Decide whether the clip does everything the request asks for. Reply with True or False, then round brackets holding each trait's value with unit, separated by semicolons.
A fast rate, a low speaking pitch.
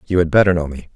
True (315 wpm; 85 Hz)